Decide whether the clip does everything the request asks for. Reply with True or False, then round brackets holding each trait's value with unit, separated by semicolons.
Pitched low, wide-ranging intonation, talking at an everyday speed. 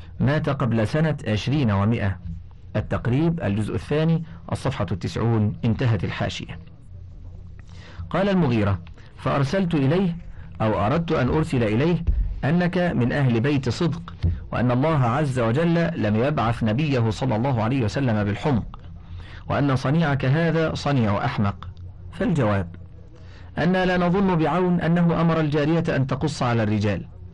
True (120 Hz; 7.4 semitones; 120 wpm)